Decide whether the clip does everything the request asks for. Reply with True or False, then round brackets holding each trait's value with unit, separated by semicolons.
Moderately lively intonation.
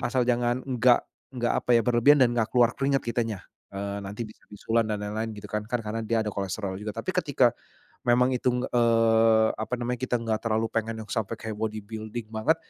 False (2.0 semitones)